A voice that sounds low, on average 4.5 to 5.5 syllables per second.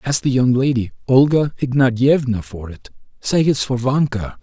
Yes: low, 125 Hz; 4.8 syllables/s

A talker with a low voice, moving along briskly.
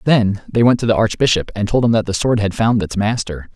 Yes: low, 105 Hz; fast, 270 wpm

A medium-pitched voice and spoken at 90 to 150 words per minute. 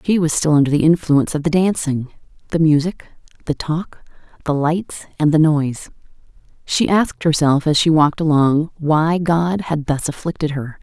No: medium, 155 Hz; average, 170 wpm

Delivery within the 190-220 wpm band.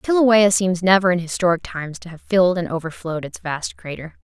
Yes: average, 200 wpm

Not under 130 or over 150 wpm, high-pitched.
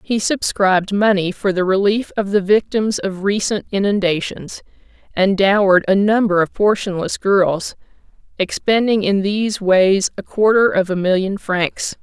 Yes: average, 145 wpm; high, 195 Hz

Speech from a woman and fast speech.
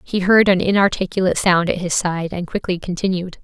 No: female; average, 190 wpm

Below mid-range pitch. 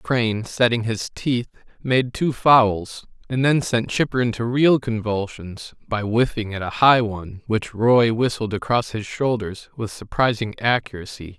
Yes: low, 115 Hz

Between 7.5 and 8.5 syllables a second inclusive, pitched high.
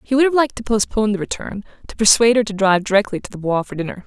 Yes: 7.8 syllables/s; high, 215 Hz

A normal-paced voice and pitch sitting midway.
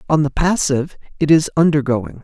Yes: average, 160 wpm; medium, 150 Hz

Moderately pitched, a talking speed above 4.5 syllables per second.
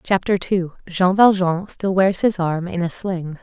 No: medium, 180 Hz; 4.1 syllables/s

